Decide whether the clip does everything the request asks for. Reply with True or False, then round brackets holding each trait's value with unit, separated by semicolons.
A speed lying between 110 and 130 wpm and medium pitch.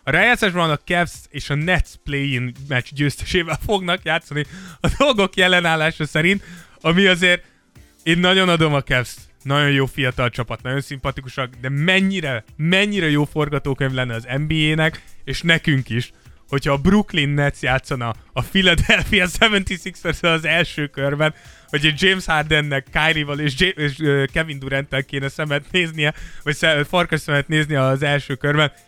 False (150 wpm; 150 Hz)